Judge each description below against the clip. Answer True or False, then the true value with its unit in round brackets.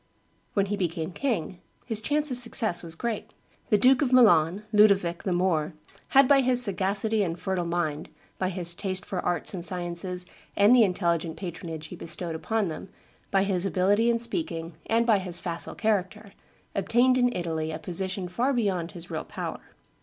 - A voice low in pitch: False (190 Hz)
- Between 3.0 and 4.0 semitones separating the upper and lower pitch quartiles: False (4.4 semitones)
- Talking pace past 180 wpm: False (175 wpm)